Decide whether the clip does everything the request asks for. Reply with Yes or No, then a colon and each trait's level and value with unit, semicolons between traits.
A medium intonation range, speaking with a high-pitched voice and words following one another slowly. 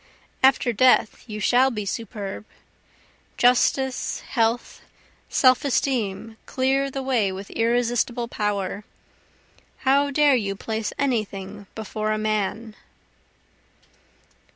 Yes: average, 3.6 semitones; high, 230 Hz; slow, 105 wpm